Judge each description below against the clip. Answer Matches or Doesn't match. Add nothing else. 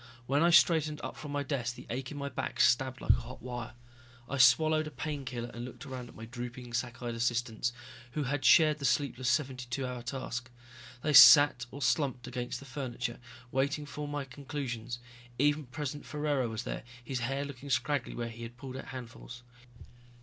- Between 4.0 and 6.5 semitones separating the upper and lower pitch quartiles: Doesn't match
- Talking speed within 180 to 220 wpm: Matches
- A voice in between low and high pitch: Doesn't match